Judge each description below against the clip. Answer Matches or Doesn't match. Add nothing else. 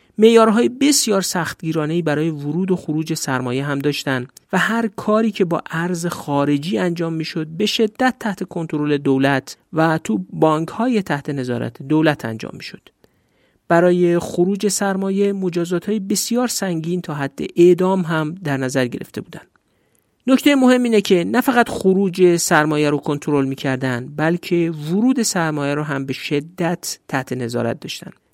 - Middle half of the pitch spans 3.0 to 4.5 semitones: Doesn't match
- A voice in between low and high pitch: Matches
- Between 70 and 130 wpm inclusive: Doesn't match